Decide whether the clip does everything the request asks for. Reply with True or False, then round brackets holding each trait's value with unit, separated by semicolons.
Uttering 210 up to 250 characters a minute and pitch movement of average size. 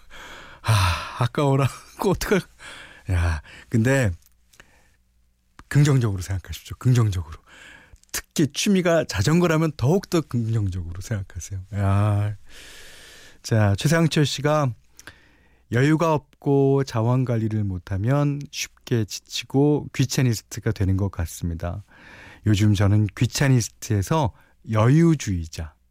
False (245 characters per minute; 6.4 semitones)